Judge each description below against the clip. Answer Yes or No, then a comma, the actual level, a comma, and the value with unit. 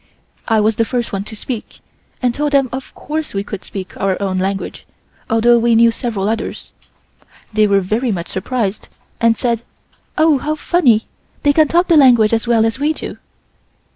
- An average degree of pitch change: Yes, average, 4.0 semitones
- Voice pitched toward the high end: Yes, high, 230 Hz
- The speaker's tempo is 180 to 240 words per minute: Yes, average, 185 wpm